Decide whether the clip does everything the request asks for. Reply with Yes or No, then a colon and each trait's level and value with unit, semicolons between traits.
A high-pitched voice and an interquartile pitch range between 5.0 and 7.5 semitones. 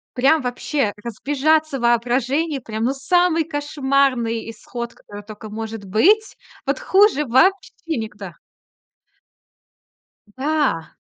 Yes: very high, 265 Hz; wide, 5.4 semitones